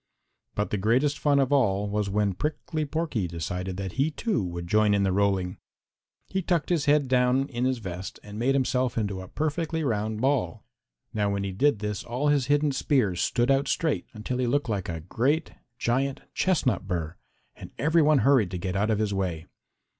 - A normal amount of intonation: No, wide, 6.3 semitones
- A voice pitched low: Yes, low, 120 Hz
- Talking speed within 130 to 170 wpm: No, average, 200 wpm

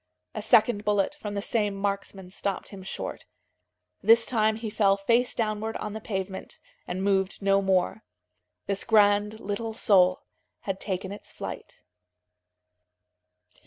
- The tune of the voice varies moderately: No, narrow, 1.9 semitones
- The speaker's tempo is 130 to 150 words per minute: Yes, slow, 135 wpm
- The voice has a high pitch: Yes, high, 205 Hz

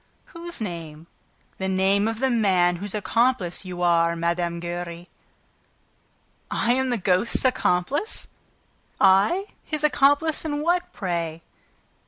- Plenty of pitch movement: Yes, wide, 6.9 semitones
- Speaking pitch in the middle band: No, high, 195 Hz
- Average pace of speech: No, slow, 120 wpm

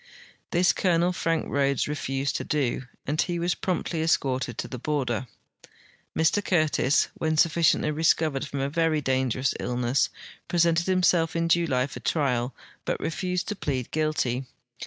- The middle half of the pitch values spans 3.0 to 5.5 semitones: Yes, average, 4.1 semitones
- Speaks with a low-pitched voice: No, medium, 155 Hz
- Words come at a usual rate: Yes, average, 145 wpm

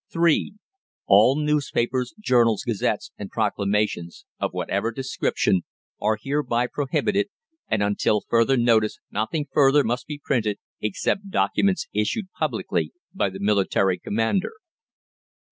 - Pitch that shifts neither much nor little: No, wide, 5.7 semitones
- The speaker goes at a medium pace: No, slow, 115 wpm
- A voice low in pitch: Yes, low, 115 Hz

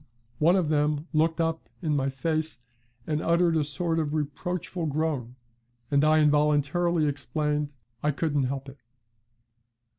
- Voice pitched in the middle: Yes, medium, 150 Hz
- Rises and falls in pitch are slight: Yes, narrow, 2.0 semitones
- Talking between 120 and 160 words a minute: Yes, average, 140 wpm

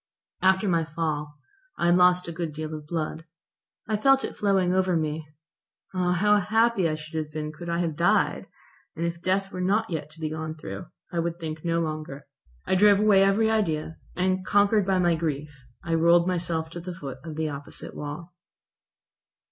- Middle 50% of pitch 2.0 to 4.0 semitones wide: Yes, average, 3.2 semitones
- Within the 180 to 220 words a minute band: Yes, average, 195 wpm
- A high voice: No, medium, 170 Hz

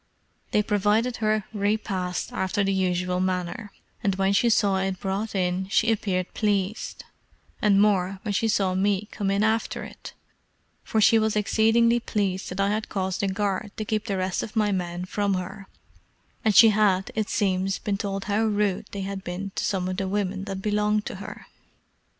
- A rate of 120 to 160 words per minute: No, average, 185 wpm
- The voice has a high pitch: Yes, high, 200 Hz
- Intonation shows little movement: Yes, narrow, 2.0 semitones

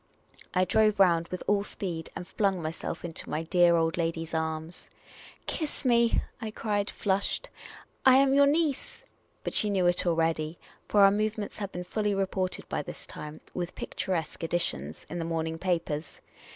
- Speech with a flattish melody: No, average, 4.0 semitones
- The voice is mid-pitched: Yes, medium, 180 Hz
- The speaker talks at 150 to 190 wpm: Yes, average, 180 wpm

